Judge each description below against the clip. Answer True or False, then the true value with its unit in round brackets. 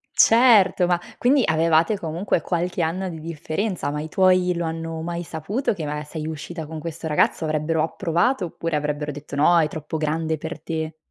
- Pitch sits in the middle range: True (165 Hz)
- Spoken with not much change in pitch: True (2.2 semitones)